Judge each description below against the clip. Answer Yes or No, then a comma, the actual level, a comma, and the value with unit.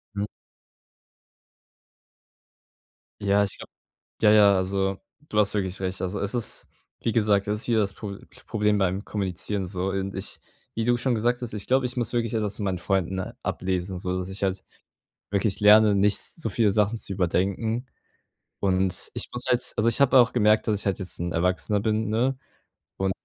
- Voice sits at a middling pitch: No, low, 100 Hz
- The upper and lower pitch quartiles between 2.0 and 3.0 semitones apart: Yes, narrow, 2.5 semitones